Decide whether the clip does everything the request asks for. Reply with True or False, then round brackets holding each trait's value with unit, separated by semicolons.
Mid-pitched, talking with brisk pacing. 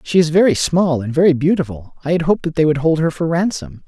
True (155 Hz; 265 wpm)